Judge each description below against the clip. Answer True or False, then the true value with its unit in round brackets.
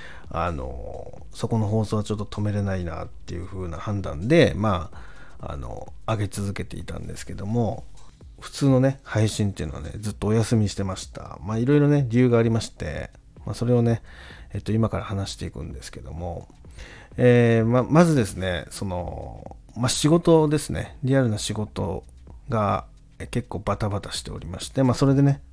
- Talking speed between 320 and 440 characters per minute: True (355 characters per minute)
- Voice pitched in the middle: False (105 Hz)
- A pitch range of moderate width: True (4.7 semitones)